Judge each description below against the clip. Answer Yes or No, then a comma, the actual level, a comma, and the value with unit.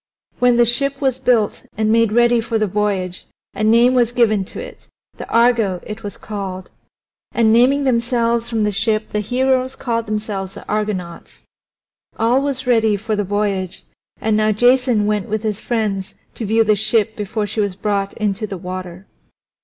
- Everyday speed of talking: Yes, average, 175 wpm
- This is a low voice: No, high, 220 Hz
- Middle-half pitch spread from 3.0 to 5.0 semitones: No, narrow, 2.5 semitones